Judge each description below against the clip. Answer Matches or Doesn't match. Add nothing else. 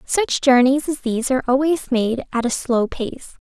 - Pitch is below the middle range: Doesn't match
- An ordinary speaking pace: Matches